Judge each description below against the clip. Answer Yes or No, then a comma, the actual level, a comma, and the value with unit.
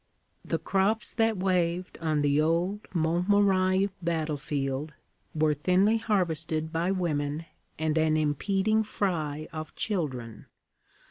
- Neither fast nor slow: No, slow, 110 wpm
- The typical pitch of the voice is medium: Yes, medium, 165 Hz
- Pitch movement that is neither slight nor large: Yes, average, 3.8 semitones